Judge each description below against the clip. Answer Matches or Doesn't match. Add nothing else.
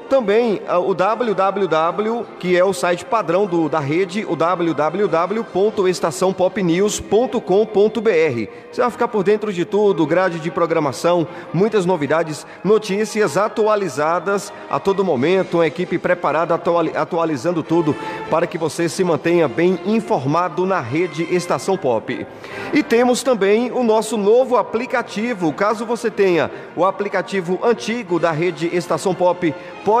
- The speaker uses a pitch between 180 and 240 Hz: Matches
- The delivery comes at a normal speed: Matches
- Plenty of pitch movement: Doesn't match